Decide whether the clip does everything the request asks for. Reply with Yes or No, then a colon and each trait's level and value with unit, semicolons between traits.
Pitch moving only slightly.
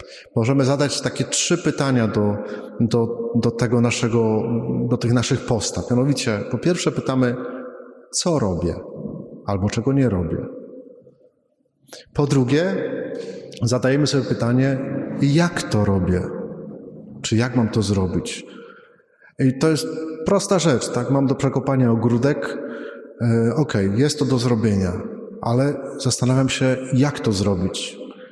No: average, 3.4 semitones